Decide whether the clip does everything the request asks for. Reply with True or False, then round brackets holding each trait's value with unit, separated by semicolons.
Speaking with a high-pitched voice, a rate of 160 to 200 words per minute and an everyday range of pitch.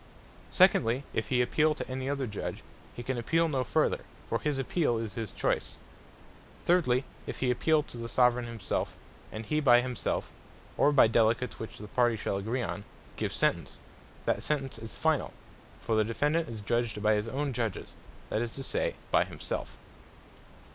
False (120 Hz; 175 wpm; 3.5 semitones)